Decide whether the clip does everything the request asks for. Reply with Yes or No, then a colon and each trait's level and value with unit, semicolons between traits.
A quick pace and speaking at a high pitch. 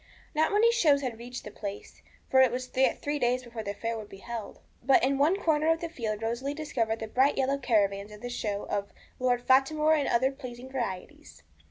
Yes: fast, 215 wpm; very high, 255 Hz